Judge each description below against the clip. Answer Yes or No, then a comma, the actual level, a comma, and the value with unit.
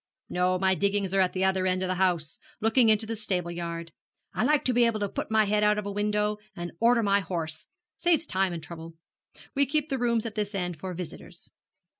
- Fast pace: Yes, fast, 225 wpm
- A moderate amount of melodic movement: Yes, average, 3.4 semitones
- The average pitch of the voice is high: Yes, high, 200 Hz